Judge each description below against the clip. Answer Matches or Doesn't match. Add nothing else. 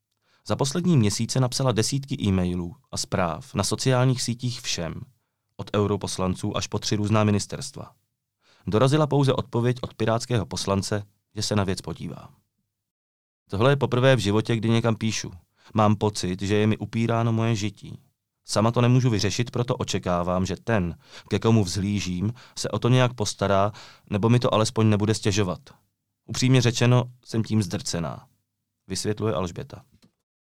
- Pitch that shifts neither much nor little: Matches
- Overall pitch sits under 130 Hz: Matches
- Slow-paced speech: Doesn't match